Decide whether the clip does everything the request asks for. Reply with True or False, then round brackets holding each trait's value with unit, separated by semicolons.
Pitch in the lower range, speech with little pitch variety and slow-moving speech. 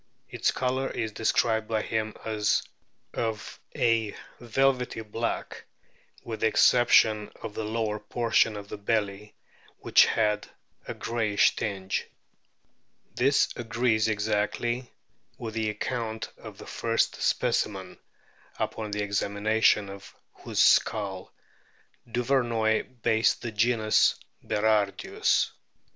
True (110 Hz; 1.8 semitones; 110 wpm)